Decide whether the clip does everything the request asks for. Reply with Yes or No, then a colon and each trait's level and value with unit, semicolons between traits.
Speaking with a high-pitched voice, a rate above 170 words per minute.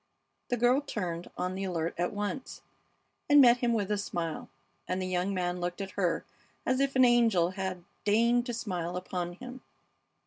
Yes: high, 195 Hz; average, 180 wpm